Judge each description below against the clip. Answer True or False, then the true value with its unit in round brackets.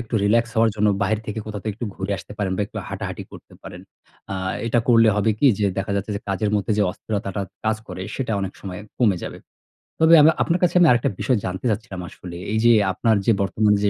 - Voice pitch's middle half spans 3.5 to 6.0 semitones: False (2.6 semitones)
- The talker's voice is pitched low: True (105 Hz)